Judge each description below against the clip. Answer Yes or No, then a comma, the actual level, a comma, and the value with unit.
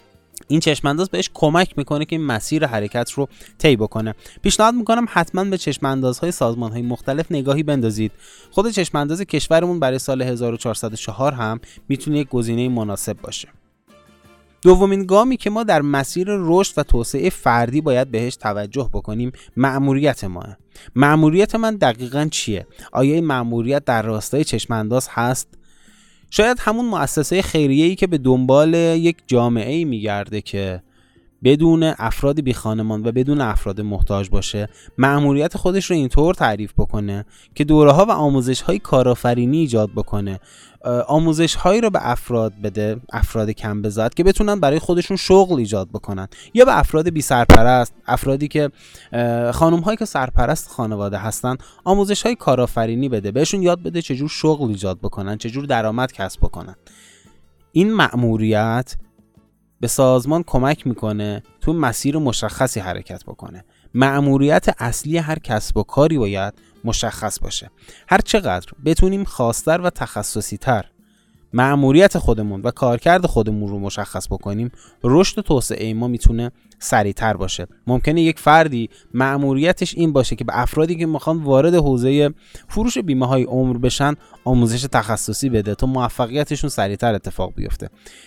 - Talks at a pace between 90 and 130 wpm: No, average, 145 wpm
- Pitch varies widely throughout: Yes, wide, 6.1 semitones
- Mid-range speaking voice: No, low, 130 Hz